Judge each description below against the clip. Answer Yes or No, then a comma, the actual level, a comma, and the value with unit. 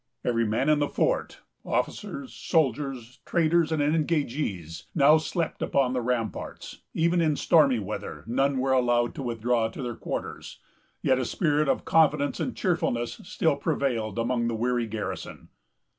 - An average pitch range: Yes, average, 4.6 semitones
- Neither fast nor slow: Yes, average, 150 wpm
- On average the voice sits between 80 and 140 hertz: Yes, low, 135 Hz